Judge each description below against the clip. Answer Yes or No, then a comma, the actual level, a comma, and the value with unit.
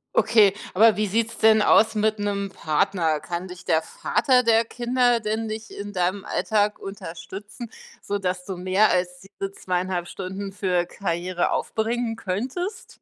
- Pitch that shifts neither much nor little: Yes, average, 3.2 semitones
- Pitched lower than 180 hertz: No, high, 200 Hz